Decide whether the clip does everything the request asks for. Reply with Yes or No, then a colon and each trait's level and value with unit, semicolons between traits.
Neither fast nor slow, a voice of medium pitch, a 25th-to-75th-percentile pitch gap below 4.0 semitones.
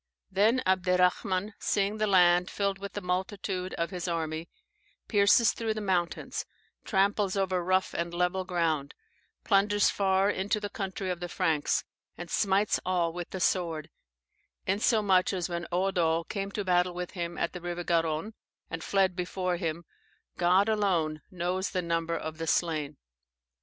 Yes: average, 155 wpm; medium, 180 Hz; narrow, 2.4 semitones